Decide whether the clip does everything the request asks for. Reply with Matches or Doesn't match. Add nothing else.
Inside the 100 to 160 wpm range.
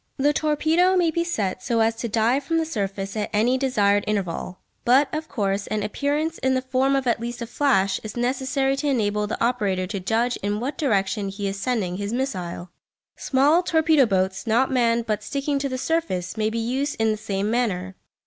Doesn't match